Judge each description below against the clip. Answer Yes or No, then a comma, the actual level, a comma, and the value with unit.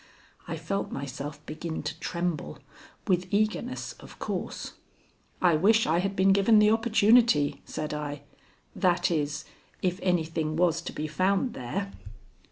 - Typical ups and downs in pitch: Yes, average, 4.6 semitones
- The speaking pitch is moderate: Yes, medium, 175 Hz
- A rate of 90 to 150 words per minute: Yes, average, 140 wpm